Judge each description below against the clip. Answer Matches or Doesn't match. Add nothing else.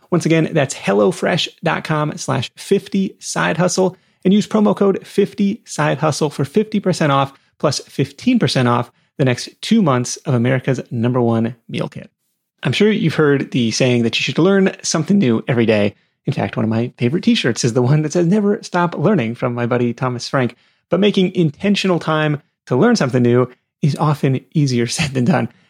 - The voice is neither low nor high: Matches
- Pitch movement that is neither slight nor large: Doesn't match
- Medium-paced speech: Matches